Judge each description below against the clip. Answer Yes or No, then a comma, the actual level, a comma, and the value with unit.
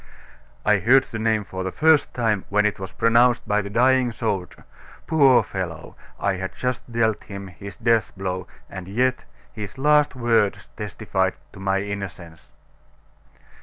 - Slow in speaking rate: No, average, 155 wpm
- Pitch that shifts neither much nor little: Yes, average, 3.9 semitones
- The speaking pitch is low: Yes, low, 105 Hz